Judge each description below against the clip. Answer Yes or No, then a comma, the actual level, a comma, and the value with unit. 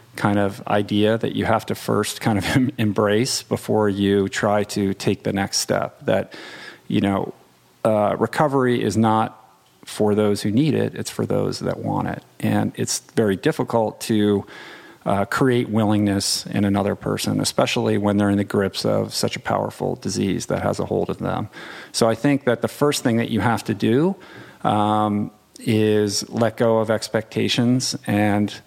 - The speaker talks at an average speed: Yes, average, 175 wpm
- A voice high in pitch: No, low, 105 Hz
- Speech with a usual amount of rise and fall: No, narrow, 2.0 semitones